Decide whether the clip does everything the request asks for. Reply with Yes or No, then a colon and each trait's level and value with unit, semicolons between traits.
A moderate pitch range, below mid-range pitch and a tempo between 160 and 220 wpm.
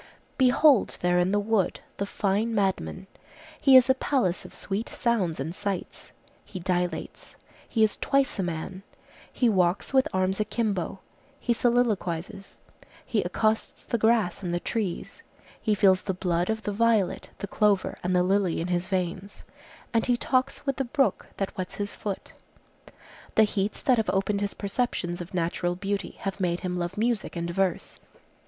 No: average, 3.8 semitones; high, 200 Hz; average, 170 wpm